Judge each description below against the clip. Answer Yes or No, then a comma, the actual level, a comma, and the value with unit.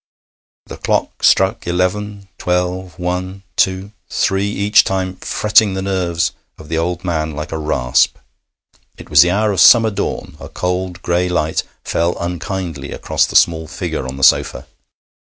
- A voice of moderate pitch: No, very low, 90 Hz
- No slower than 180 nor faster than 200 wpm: No, average, 155 wpm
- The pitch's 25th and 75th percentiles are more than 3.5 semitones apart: No, narrow, 2.6 semitones